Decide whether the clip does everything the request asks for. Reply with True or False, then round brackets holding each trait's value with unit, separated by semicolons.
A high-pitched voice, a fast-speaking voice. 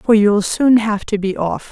True (210 Hz; 245 wpm)